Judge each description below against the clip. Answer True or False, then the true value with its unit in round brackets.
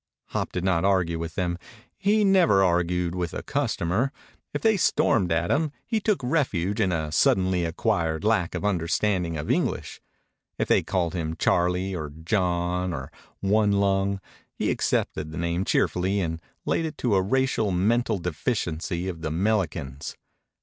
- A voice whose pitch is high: False (90 Hz)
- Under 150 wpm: False (160 wpm)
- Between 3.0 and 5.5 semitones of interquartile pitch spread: True (3.8 semitones)